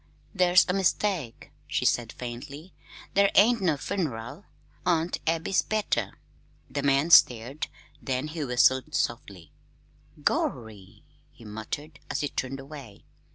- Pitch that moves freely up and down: Yes, wide, 6.2 semitones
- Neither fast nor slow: No, slow, 120 wpm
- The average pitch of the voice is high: No, medium, 140 Hz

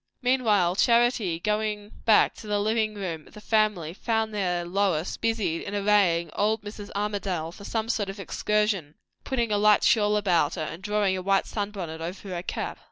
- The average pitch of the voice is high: Yes, high, 205 Hz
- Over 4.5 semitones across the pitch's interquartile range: No, average, 3.0 semitones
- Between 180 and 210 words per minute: Yes, average, 185 wpm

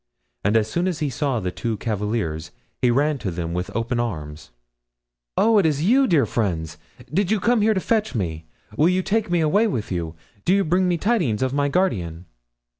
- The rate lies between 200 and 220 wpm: Yes, fast, 205 wpm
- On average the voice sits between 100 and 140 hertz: Yes, low, 135 Hz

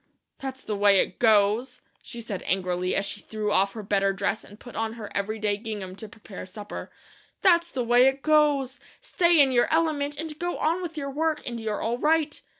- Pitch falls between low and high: No, high, 235 Hz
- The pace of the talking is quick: Yes, fast, 210 wpm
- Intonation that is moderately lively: No, wide, 6.2 semitones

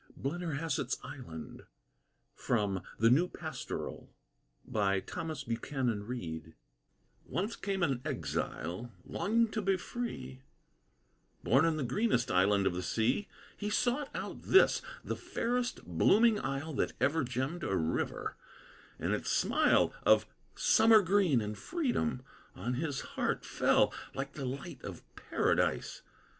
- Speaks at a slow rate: Yes, slow, 120 wpm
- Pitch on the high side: No, low, 135 Hz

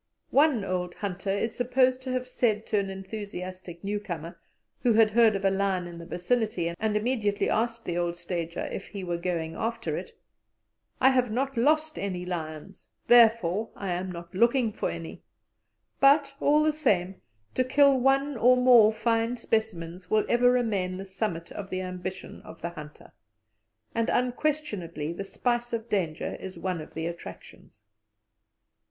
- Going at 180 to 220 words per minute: No, average, 165 wpm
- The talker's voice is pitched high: Yes, high, 205 Hz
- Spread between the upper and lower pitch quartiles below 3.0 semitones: No, average, 5.3 semitones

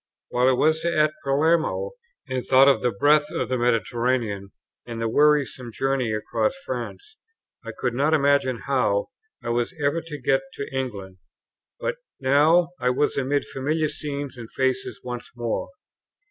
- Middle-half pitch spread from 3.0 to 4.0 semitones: Yes, average, 3.5 semitones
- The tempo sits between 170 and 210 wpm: No, average, 155 wpm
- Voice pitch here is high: No, low, 135 Hz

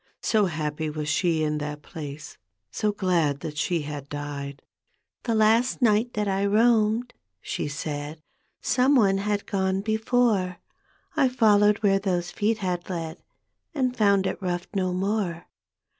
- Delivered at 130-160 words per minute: Yes, average, 155 wpm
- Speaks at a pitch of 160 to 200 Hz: Yes, high, 190 Hz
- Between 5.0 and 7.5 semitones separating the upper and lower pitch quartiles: Yes, wide, 5.5 semitones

